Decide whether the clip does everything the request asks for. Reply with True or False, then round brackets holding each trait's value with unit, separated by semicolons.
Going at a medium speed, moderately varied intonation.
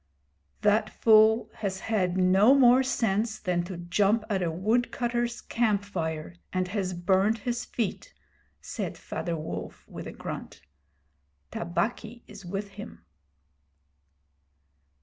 False (120 wpm; 3.7 semitones)